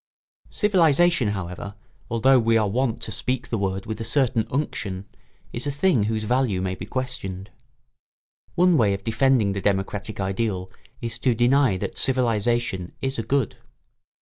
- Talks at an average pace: Yes, average, 160 wpm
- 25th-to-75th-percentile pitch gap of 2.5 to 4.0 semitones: No, average, 4.8 semitones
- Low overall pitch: Yes, low, 115 Hz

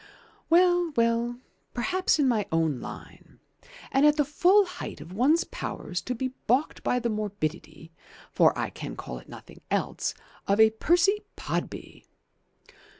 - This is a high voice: Yes, high, 245 Hz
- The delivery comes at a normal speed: Yes, average, 150 wpm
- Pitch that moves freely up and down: Yes, wide, 8.2 semitones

